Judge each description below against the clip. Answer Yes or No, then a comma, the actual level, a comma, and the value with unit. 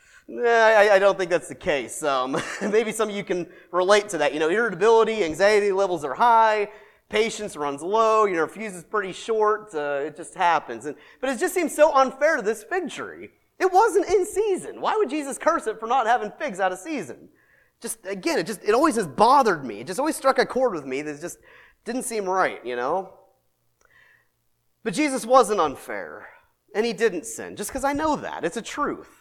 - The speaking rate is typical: No, fast, 215 wpm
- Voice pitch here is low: No, high, 220 Hz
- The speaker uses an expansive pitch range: Yes, wide, 6.2 semitones